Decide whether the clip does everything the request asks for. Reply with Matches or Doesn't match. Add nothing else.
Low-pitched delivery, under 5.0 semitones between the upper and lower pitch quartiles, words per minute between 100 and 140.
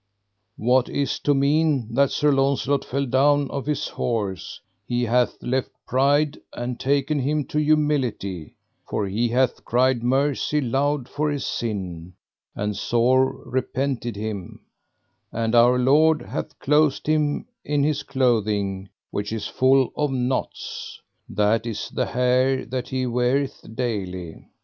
Matches